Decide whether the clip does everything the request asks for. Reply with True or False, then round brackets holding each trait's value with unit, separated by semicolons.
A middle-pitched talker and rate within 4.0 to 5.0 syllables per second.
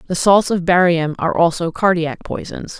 False (170 Hz; 5.2 syllables/s)